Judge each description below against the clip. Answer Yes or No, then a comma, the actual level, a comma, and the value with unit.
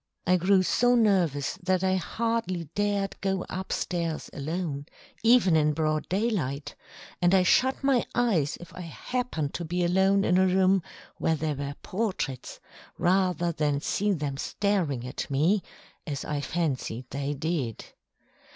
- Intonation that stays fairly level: No, average, 4.6 semitones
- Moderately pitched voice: Yes, medium, 175 Hz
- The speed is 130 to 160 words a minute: Yes, average, 150 wpm